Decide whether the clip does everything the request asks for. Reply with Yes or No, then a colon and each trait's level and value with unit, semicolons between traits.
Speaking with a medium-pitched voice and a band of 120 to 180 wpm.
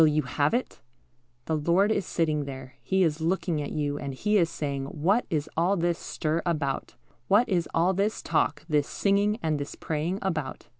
No: medium, 160 Hz; average, 195 wpm